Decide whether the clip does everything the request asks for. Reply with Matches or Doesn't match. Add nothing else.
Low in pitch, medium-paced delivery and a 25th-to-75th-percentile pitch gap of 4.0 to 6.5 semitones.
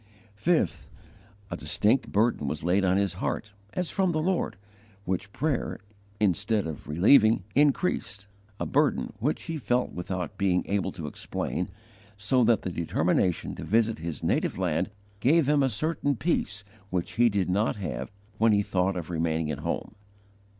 Matches